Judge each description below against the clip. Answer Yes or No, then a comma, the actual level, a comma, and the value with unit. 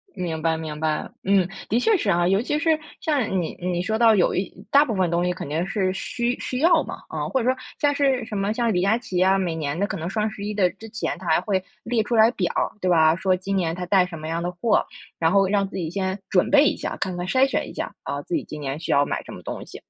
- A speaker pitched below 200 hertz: Yes, high, 190 Hz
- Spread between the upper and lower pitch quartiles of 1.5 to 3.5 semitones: No, average, 4.4 semitones